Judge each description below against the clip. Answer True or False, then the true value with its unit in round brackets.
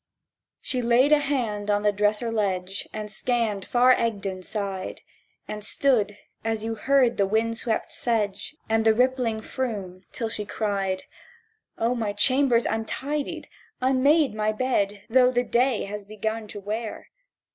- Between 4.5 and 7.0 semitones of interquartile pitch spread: False (3.2 semitones)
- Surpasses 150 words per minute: False (145 wpm)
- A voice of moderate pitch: False (220 Hz)